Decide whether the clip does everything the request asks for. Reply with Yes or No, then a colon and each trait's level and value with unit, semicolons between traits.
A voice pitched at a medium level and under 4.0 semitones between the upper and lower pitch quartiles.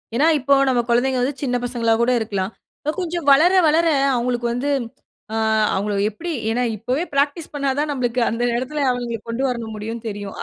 No: high, 245 Hz; average, 3.5 semitones